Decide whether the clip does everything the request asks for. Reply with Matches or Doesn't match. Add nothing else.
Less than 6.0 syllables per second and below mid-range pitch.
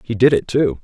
Matches